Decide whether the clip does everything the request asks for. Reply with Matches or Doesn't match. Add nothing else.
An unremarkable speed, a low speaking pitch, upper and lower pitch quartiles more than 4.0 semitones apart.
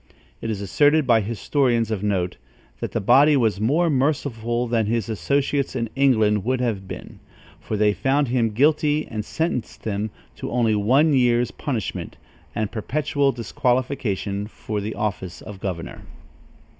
Matches